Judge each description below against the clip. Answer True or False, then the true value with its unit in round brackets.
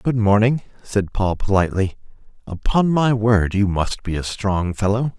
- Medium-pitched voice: False (105 Hz)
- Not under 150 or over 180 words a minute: True (160 wpm)